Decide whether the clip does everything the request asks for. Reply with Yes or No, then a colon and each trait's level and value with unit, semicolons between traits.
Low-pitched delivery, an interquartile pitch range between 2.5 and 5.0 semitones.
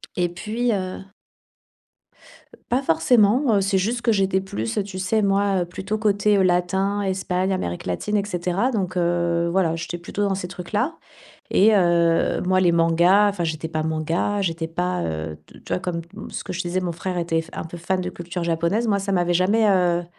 No: medium, 185 Hz; average, 2.8 semitones